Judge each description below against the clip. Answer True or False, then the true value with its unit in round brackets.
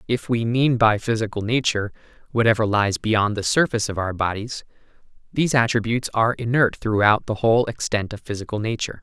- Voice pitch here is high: False (110 Hz)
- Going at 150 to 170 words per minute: True (165 wpm)